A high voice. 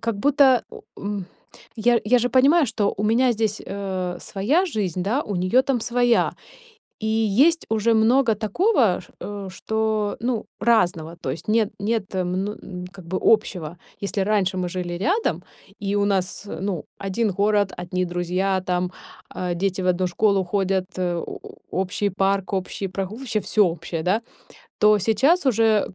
Yes: high, 200 Hz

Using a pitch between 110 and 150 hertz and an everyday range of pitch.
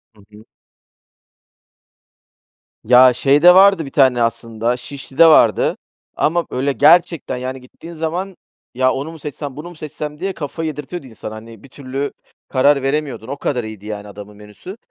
Yes: low, 135 Hz; average, 4.4 semitones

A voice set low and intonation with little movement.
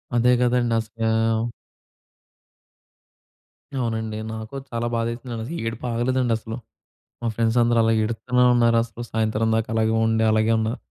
Yes: low, 115 Hz; narrow, 1.1 semitones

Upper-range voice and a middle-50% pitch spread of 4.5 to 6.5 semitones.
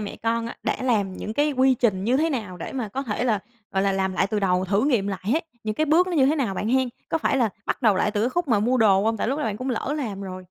Yes: high, 225 Hz; average, 4.9 semitones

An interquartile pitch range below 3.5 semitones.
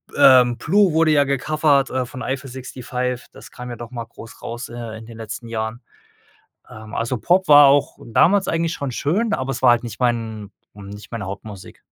No: average, 3.8 semitones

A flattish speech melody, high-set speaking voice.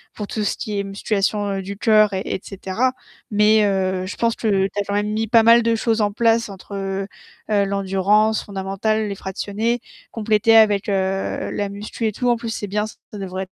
Yes: narrow, 2.0 semitones; high, 205 Hz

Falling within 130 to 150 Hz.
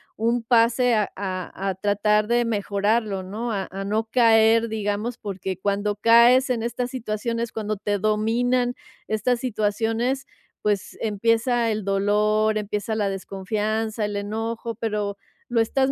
No: high, 215 Hz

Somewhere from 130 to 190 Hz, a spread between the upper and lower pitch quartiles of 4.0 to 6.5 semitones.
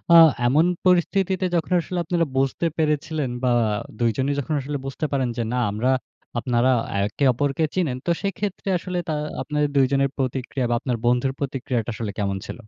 Yes: medium, 140 Hz; average, 4.6 semitones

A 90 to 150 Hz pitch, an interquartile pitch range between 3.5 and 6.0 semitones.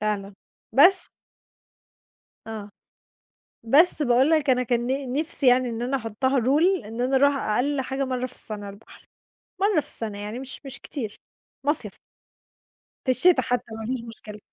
No: very high, 255 Hz; average, 3.8 semitones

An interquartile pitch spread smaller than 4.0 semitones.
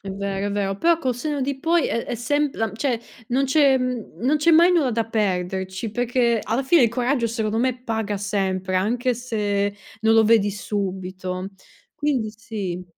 No: average, 4.3 semitones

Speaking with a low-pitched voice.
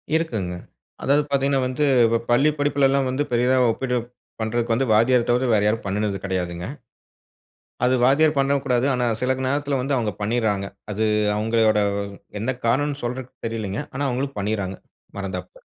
Yes: low, 125 Hz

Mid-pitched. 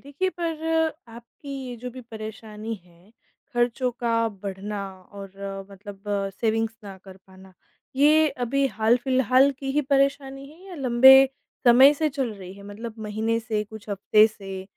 No: high, 230 Hz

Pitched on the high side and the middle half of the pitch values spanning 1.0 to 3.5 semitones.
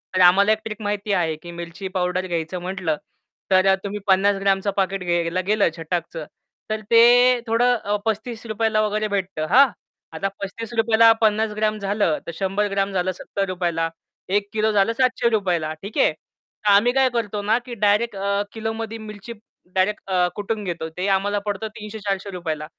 Yes: high, 200 Hz; average, 2.8 semitones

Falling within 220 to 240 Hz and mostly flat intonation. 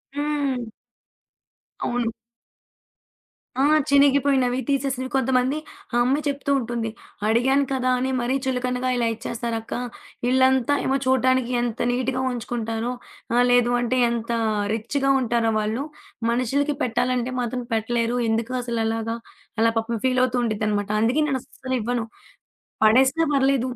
No: very high, 250 Hz; narrow, 2.2 semitones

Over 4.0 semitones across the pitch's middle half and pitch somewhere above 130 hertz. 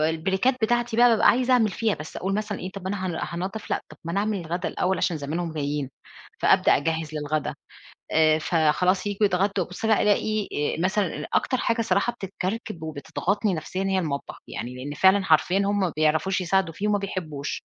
Yes: average, 4.4 semitones; medium, 185 Hz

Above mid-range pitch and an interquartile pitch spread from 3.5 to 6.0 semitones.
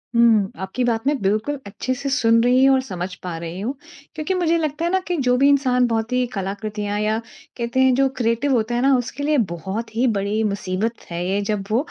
Yes: high, 230 Hz; average, 4.5 semitones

